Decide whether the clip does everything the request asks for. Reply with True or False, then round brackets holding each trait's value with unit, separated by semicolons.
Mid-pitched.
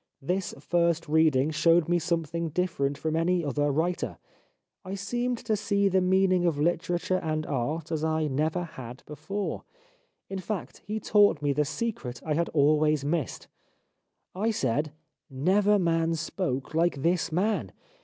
True (165 Hz)